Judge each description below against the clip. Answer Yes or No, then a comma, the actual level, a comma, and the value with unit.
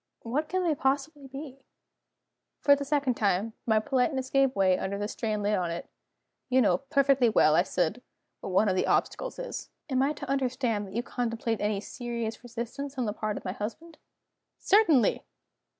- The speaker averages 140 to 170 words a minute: No, average, 180 wpm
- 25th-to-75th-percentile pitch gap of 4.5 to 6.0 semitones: Yes, average, 4.8 semitones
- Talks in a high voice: Yes, high, 240 Hz